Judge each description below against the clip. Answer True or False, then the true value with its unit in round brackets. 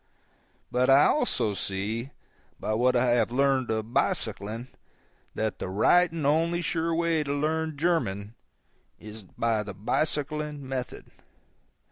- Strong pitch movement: True (6.1 semitones)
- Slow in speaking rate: True (130 wpm)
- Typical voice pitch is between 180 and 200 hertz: False (130 Hz)